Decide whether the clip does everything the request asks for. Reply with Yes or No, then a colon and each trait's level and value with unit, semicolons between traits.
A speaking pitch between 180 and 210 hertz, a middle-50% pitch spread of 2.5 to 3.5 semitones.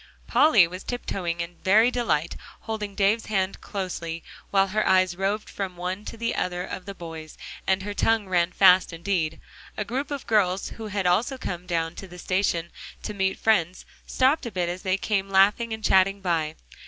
Yes: high, 190 Hz; average, 3.1 semitones